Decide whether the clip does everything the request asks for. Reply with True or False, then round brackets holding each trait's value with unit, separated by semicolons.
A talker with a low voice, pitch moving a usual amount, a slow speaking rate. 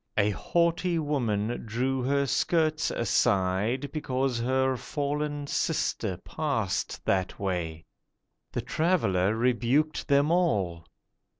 False (130 Hz; 6.5 semitones; 100 wpm)